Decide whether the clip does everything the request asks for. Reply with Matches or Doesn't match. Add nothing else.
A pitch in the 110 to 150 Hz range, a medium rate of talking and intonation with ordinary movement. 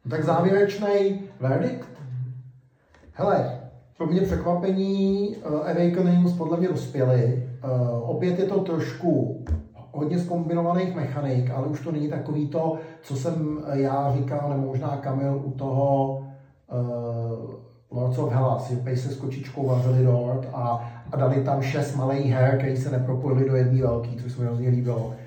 Matches